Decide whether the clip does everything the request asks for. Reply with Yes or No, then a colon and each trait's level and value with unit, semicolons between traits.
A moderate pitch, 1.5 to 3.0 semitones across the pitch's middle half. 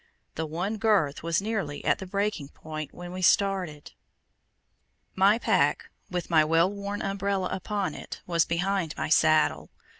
No: medium, 180 Hz; average, 3.9 semitones